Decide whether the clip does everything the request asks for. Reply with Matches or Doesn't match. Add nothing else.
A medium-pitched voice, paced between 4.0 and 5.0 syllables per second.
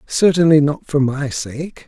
Matches